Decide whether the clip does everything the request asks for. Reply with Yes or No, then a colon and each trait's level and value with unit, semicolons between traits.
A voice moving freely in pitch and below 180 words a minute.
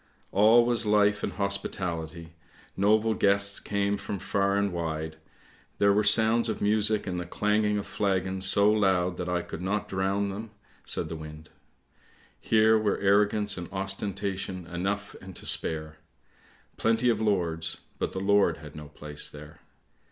No: average, 2.8 semitones; average, 165 wpm